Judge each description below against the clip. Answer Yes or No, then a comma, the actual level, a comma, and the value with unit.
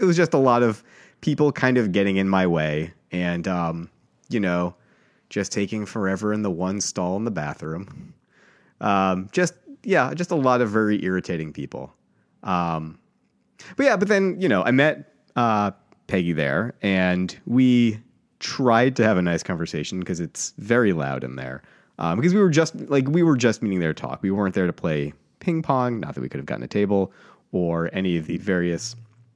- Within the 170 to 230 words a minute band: Yes, average, 195 wpm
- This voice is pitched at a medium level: No, low, 100 Hz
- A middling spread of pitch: No, wide, 6.0 semitones